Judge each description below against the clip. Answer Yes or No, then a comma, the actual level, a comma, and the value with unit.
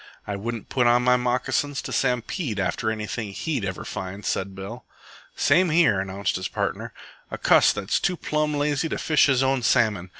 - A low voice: Yes, low, 120 Hz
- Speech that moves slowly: No, average, 180 wpm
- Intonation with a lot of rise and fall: Yes, wide, 6.1 semitones